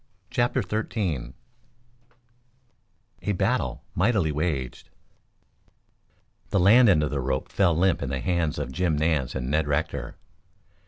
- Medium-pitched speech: No, very low, 80 Hz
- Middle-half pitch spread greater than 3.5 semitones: Yes, average, 5.2 semitones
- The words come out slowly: Yes, slow, 125 wpm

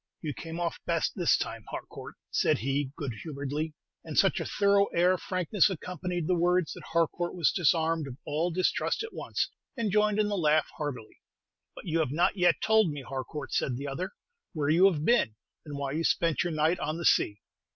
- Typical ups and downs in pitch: Yes, average, 3.7 semitones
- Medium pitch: Yes, medium, 165 Hz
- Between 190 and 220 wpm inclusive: Yes, fast, 205 wpm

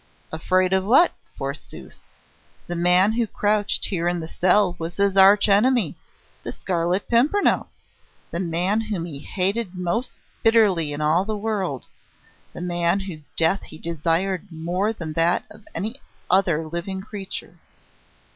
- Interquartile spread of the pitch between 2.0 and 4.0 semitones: Yes, average, 3.5 semitones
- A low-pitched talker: No, medium, 185 Hz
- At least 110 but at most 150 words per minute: Yes, average, 145 wpm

